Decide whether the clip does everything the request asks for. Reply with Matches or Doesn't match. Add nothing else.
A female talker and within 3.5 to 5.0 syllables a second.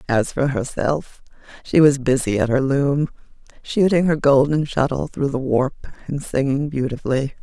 Matches